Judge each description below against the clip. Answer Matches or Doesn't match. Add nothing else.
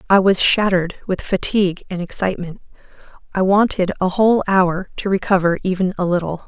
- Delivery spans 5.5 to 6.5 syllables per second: Matches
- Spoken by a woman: Matches